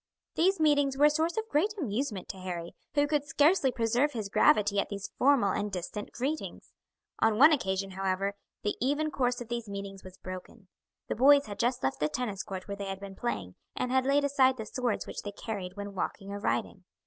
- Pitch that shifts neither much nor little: No, wide, 6.1 semitones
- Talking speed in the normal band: No, fast, 210 wpm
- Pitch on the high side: Yes, high, 225 Hz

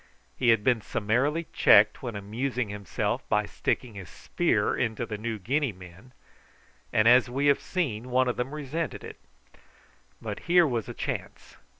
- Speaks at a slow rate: No, average, 165 wpm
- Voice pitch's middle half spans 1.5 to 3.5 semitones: No, average, 4.2 semitones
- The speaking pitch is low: Yes, low, 120 Hz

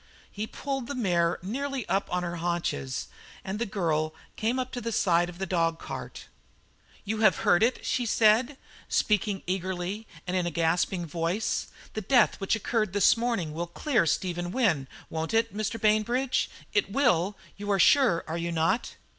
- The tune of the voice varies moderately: Yes, average, 4.9 semitones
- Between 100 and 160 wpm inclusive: No, average, 175 wpm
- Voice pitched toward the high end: Yes, high, 195 Hz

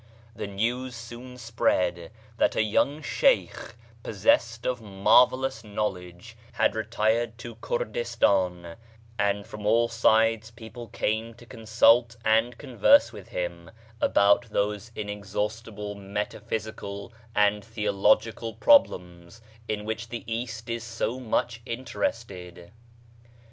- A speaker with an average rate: No, slow, 115 wpm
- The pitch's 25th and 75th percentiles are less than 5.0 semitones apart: Yes, narrow, 2.5 semitones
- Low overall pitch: Yes, low, 110 Hz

